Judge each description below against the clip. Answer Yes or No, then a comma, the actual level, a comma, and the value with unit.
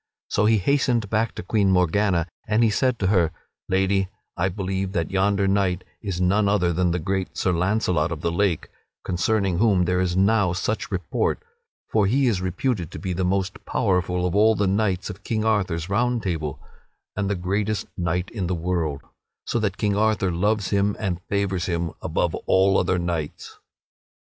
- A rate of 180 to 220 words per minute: Yes, average, 185 wpm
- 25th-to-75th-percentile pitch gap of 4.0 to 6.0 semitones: No, average, 2.7 semitones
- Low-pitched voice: Yes, very low, 95 Hz